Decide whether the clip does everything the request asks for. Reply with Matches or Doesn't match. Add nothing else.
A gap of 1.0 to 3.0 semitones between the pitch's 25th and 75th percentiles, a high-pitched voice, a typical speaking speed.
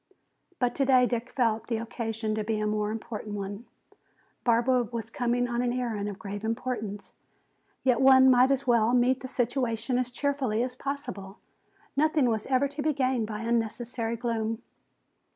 Matches